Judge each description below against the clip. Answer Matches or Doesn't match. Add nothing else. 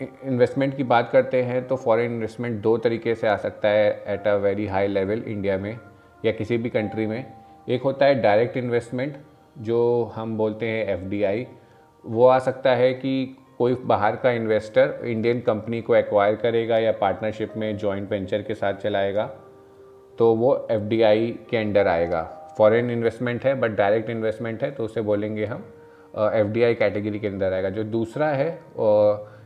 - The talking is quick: Doesn't match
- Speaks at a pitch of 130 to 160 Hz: Doesn't match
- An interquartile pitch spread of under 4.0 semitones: Matches